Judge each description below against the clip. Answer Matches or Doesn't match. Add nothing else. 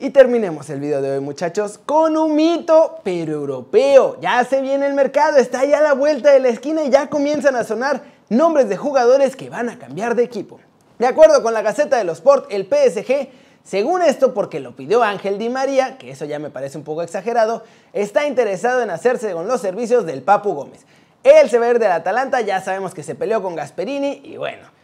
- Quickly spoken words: Matches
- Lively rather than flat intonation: Matches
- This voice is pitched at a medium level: Doesn't match